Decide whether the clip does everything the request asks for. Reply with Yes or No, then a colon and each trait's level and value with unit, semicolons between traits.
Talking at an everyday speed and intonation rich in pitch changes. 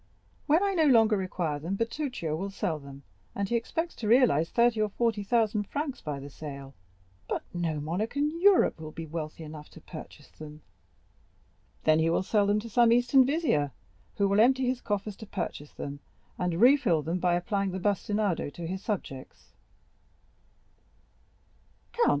Yes: average, 170 wpm; wide, 6.8 semitones